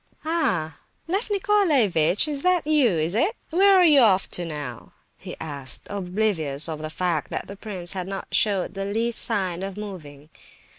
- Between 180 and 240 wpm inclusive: No, average, 165 wpm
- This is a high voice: Yes, high, 195 Hz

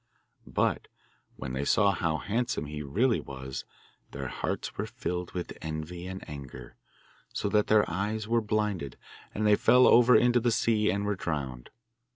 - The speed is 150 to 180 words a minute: Yes, average, 165 wpm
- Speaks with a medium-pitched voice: No, low, 100 Hz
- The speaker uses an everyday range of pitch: No, wide, 6.2 semitones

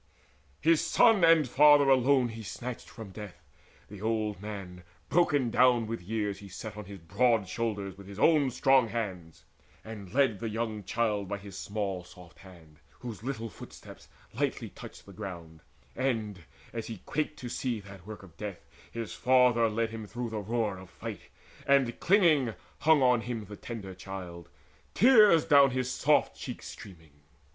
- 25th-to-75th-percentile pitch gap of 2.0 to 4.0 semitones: No, average, 4.4 semitones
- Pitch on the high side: No, low, 110 Hz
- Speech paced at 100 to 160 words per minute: No, average, 170 wpm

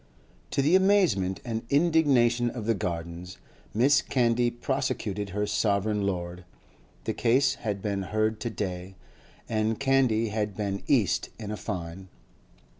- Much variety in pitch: No, average, 3.8 semitones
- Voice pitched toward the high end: No, low, 110 Hz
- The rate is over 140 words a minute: No, slow, 135 wpm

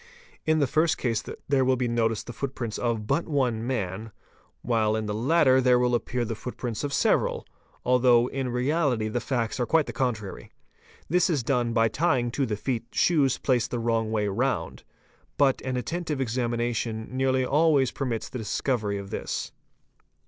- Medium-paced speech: Yes, average, 175 wpm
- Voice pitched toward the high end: No, low, 125 Hz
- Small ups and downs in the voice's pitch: No, average, 3.0 semitones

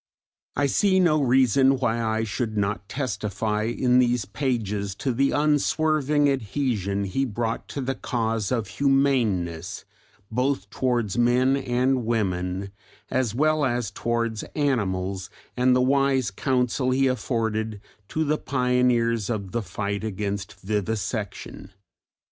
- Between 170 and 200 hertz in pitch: No, low, 120 Hz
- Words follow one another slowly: Yes, slow, 125 wpm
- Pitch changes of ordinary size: Yes, average, 4.3 semitones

